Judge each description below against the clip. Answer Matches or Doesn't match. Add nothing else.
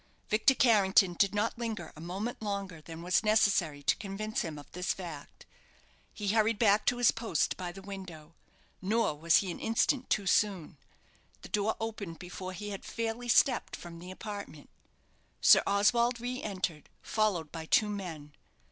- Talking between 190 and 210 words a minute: Doesn't match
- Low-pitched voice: Doesn't match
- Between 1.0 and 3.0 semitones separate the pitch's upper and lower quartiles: Doesn't match